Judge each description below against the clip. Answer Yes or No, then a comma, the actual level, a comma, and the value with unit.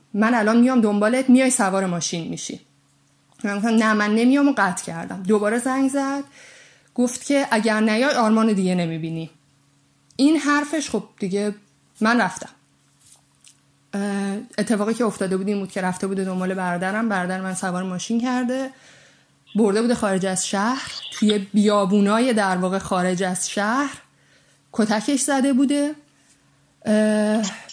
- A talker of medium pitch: No, high, 215 Hz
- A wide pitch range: No, average, 4.4 semitones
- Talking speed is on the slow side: No, average, 140 wpm